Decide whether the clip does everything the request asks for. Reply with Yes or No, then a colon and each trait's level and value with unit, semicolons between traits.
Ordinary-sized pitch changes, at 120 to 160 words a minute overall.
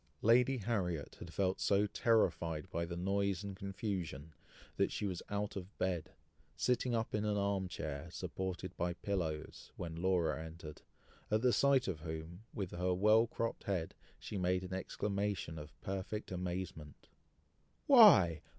Yes: average, 3.4 semitones; average, 150 wpm